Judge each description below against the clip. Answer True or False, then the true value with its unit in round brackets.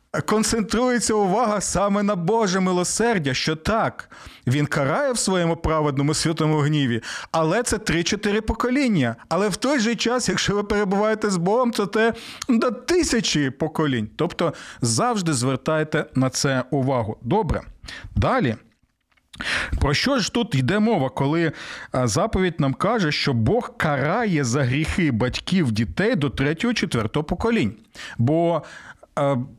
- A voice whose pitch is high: False (170 Hz)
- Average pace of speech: True (130 wpm)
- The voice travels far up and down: True (7.3 semitones)